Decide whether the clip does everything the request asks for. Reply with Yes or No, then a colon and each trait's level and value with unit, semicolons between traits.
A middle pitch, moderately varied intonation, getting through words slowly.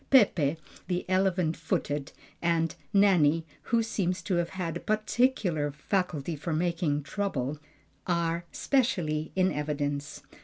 Yes: medium, 170 Hz; average, 4.0 semitones; slow, 120 wpm